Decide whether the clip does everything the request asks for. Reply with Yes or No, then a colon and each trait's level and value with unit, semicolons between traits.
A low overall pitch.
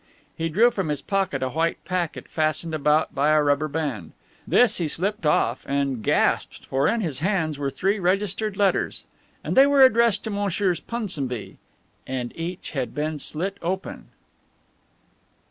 No: medium, 165 Hz